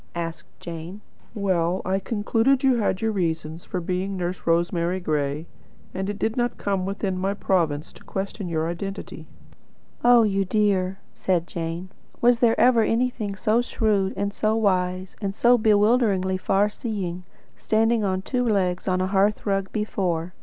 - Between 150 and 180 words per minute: Yes, average, 160 wpm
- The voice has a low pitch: No, high, 195 Hz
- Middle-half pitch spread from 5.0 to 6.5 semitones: No, average, 3.1 semitones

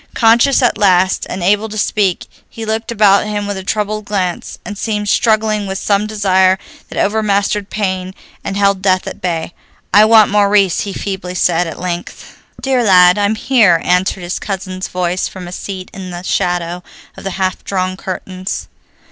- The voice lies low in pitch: No, high, 195 Hz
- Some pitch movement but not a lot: No, narrow, 2.3 semitones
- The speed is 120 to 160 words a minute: No, average, 175 wpm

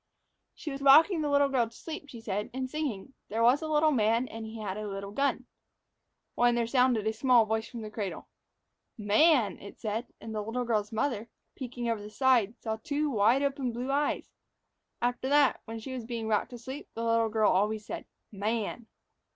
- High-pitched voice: Yes, high, 235 Hz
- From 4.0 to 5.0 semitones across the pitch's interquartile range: No, average, 3.5 semitones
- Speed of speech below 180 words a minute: No, average, 200 wpm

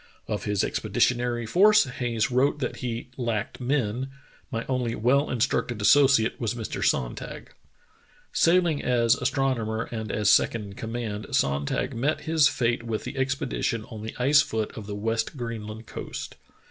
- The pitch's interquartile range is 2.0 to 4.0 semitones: Yes, average, 3.2 semitones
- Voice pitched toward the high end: No, low, 120 Hz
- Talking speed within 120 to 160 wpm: Yes, average, 155 wpm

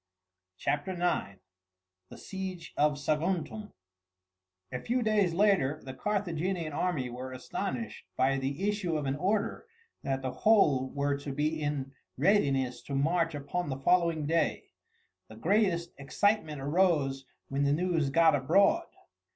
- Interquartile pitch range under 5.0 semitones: No, average, 5.3 semitones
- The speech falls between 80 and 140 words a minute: Yes, slow, 135 wpm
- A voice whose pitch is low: No, medium, 155 Hz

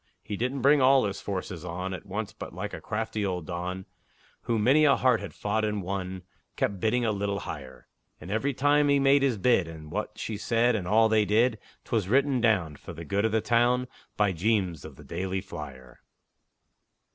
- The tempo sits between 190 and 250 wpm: Yes, fast, 205 wpm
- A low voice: Yes, low, 105 Hz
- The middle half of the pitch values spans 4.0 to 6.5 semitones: Yes, average, 4.4 semitones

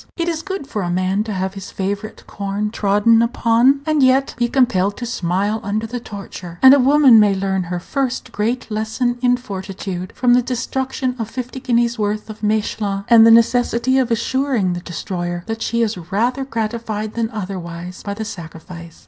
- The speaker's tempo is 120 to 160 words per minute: No, average, 185 wpm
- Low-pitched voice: No, high, 220 Hz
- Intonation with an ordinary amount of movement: Yes, average, 3.9 semitones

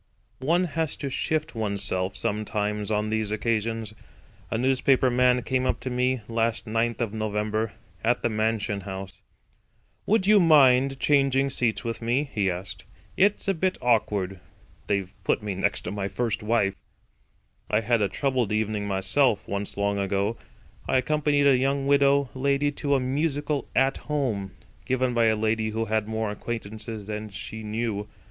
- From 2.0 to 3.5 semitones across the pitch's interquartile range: No, average, 4.3 semitones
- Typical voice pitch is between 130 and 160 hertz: No, low, 115 Hz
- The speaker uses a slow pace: No, average, 160 wpm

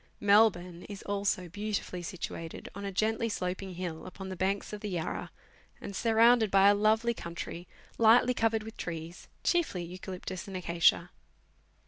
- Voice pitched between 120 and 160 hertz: No, high, 195 Hz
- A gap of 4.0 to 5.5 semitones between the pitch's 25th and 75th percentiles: No, average, 3.4 semitones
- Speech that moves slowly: No, average, 150 wpm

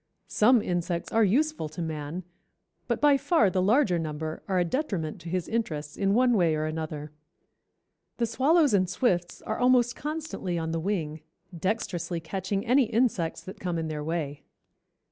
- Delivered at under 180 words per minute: Yes, average, 165 wpm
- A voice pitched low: No, medium, 185 Hz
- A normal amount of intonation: No, wide, 6.3 semitones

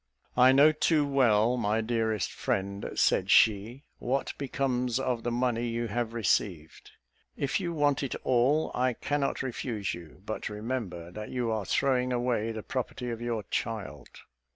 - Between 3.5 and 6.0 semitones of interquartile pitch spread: No, average, 3.1 semitones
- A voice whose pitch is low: Yes, low, 120 Hz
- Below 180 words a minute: Yes, average, 155 wpm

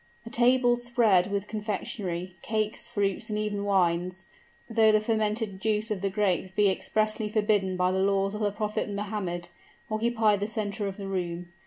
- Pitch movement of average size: No, narrow, 2.2 semitones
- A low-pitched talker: No, high, 205 Hz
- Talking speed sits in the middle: Yes, average, 170 wpm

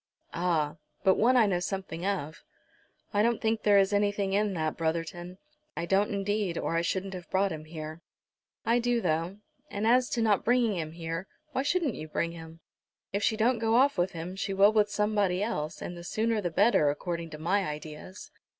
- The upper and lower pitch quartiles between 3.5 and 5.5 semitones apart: Yes, average, 4.2 semitones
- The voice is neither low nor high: No, high, 195 Hz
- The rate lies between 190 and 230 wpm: Yes, average, 200 wpm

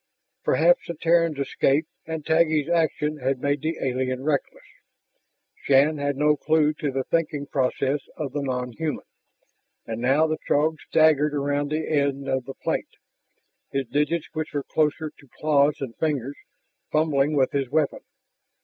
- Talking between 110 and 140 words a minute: No, average, 155 wpm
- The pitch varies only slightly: Yes, narrow, 2.3 semitones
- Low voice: No, medium, 145 Hz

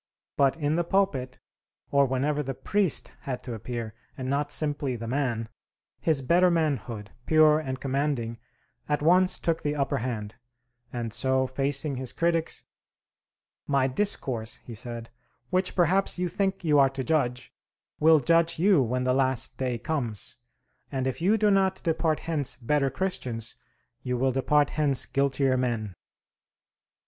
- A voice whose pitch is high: No, medium, 140 Hz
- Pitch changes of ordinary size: Yes, average, 4.1 semitones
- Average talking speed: Yes, average, 150 wpm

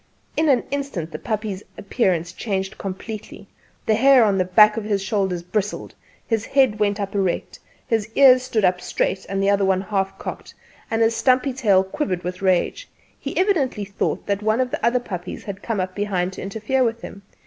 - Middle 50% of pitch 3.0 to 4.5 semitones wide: Yes, average, 3.4 semitones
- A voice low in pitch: No, high, 205 Hz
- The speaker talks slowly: No, average, 190 wpm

